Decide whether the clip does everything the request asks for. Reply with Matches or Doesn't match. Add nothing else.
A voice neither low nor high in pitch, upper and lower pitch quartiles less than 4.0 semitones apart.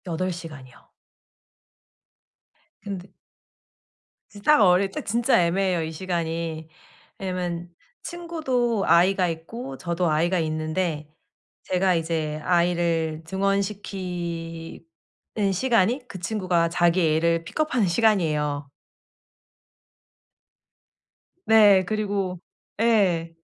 Matches